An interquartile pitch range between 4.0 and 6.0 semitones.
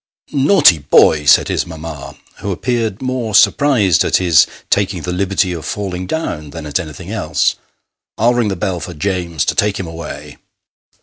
Yes: average, 4.6 semitones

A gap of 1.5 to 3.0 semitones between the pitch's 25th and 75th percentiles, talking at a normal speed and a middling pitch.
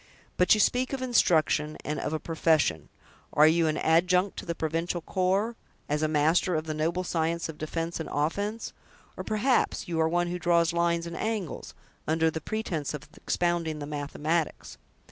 Yes: narrow, 2.5 semitones; average, 180 wpm; medium, 165 Hz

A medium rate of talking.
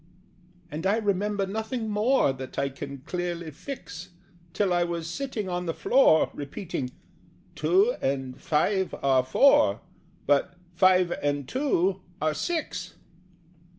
No: slow, 125 wpm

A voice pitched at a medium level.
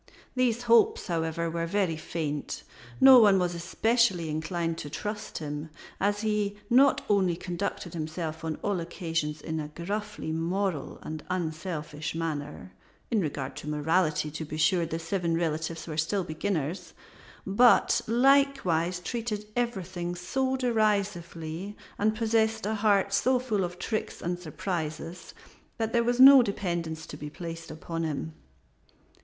Yes: medium, 175 Hz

